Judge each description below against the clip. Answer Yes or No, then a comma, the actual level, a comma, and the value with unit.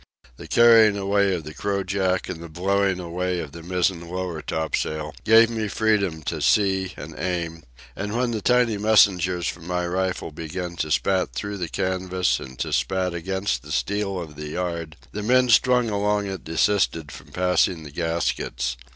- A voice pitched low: Yes, very low, 90 Hz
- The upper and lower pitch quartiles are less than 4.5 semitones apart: Yes, average, 3.4 semitones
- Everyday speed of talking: Yes, average, 175 wpm